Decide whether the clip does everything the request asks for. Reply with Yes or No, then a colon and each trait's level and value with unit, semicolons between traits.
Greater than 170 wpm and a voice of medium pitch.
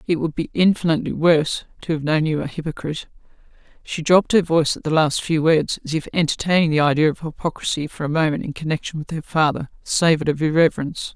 Yes: fast, 205 wpm; medium, 160 Hz